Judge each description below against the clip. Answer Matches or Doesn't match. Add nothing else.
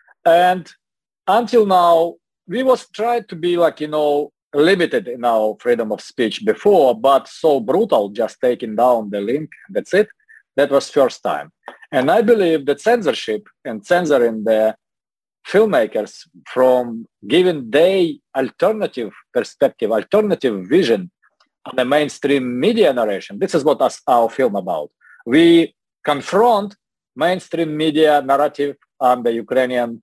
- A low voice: Doesn't match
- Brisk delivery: Doesn't match